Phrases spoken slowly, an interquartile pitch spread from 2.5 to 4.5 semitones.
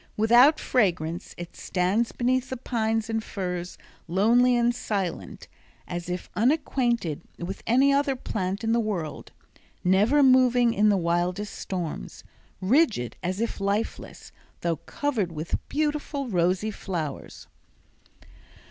No: slow, 120 wpm; wide, 5.4 semitones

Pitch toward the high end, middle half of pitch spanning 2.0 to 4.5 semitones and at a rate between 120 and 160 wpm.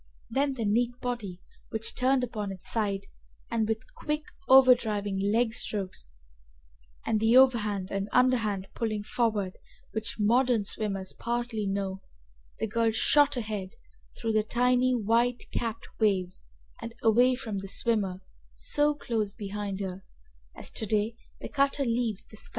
Yes: high, 220 Hz; average, 3.3 semitones; average, 140 wpm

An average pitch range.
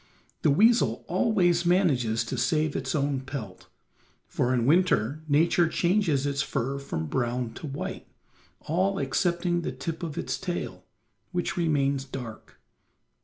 Yes: average, 5.0 semitones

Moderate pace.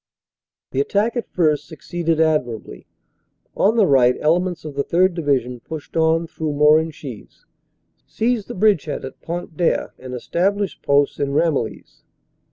Yes: average, 150 wpm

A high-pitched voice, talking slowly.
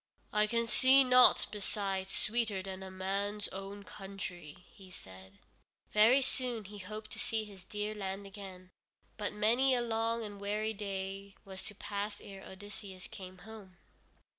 No: high, 205 Hz; average, 155 wpm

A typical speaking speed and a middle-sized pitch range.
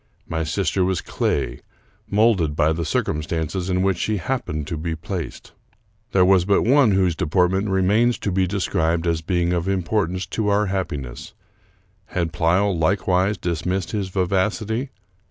Yes: average, 155 wpm; average, 3.0 semitones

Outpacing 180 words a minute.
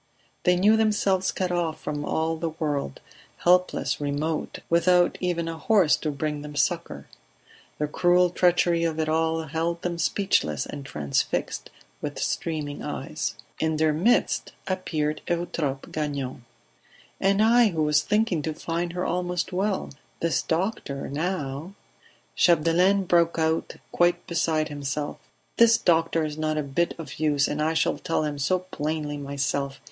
No: average, 150 wpm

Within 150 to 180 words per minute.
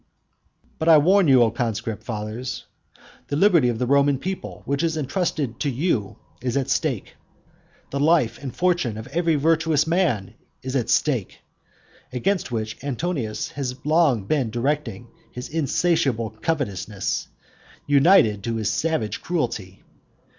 No: average, 140 wpm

